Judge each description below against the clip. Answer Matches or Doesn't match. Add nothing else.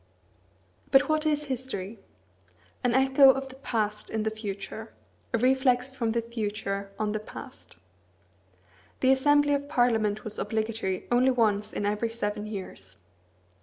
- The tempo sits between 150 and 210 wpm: Doesn't match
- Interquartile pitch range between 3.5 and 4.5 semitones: Matches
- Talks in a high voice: Matches